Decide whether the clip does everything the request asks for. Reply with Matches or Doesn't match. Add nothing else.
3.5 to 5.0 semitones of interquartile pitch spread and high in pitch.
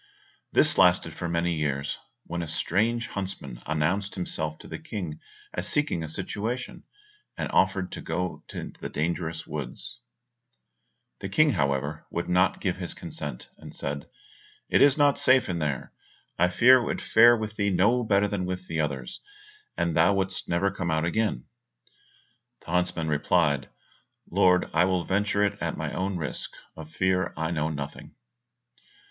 Doesn't match